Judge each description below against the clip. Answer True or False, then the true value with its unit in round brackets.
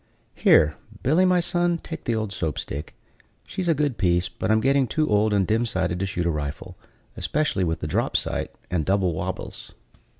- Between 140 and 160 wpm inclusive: False (195 wpm)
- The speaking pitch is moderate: False (105 Hz)